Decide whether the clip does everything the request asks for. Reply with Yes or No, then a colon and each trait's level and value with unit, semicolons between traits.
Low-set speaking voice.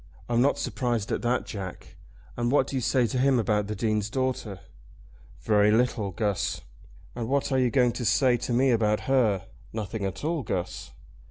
Yes: low, 120 Hz